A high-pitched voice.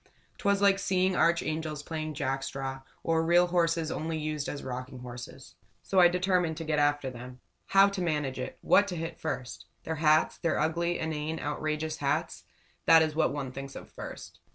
No: medium, 155 Hz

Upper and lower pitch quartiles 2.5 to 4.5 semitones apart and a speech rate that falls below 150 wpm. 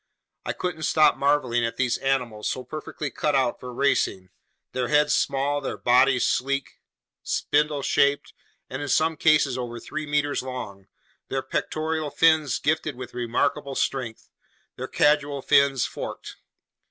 Yes: average, 2.9 semitones; average, 140 wpm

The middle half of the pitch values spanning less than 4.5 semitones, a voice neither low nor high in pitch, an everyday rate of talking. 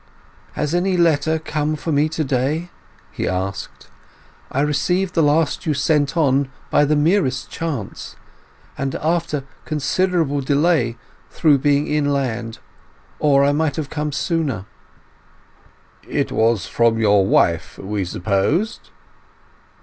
No: average, 3.8 semitones; medium, 145 Hz; slow, 120 wpm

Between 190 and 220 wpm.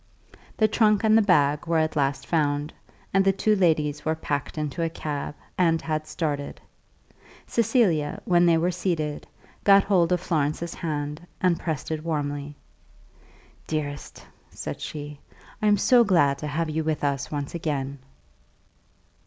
No: average, 155 wpm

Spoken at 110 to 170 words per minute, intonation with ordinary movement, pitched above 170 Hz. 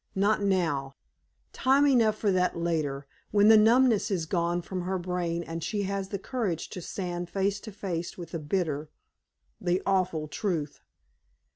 Yes: average, 160 wpm; average, 3.3 semitones; medium, 185 Hz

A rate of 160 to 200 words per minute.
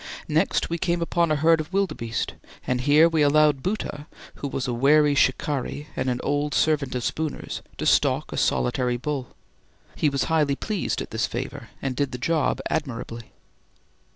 Yes: average, 175 wpm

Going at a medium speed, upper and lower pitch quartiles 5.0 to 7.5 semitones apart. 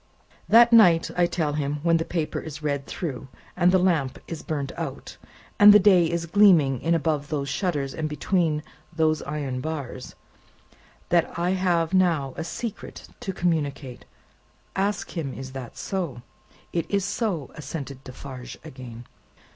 No: average, 155 wpm; average, 4.3 semitones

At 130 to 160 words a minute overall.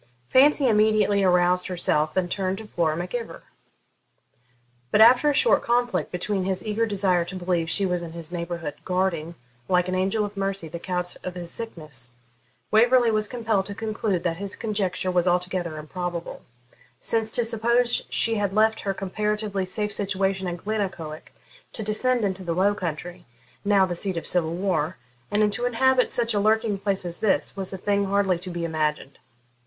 No: average, 180 wpm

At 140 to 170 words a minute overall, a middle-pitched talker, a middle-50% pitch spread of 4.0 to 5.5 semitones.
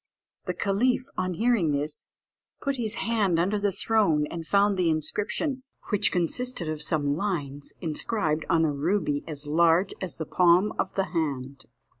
Yes: average, 160 wpm; medium, 175 Hz; average, 5.0 semitones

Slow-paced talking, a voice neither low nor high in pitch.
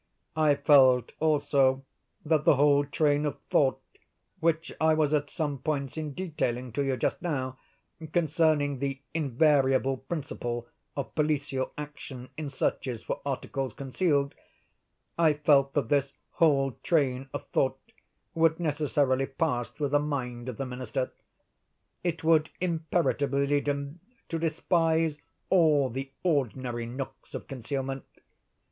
Yes: slow, 130 wpm; medium, 145 Hz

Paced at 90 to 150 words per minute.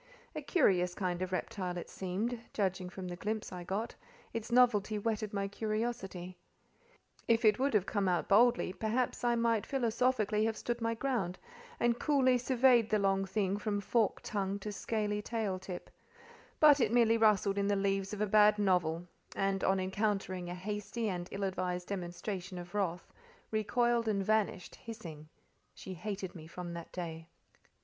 No: average, 170 wpm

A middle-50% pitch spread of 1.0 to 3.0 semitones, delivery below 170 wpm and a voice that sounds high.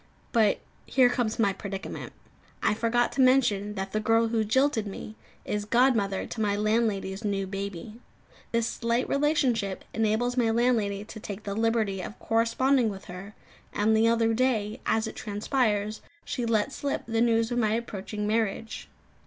Yes: narrow, 2.4 semitones; average, 160 wpm; high, 220 Hz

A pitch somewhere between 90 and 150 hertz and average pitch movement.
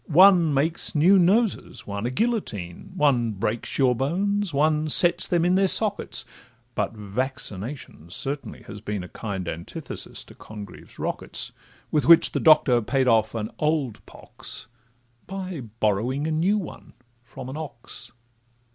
No: medium, 140 Hz; wide, 7.5 semitones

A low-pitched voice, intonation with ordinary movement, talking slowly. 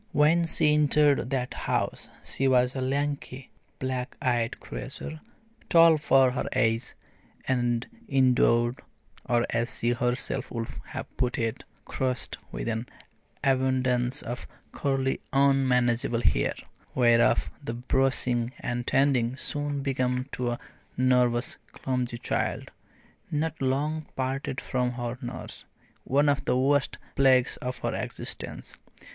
No: low, 130 Hz; narrow, 1.9 semitones; slow, 125 wpm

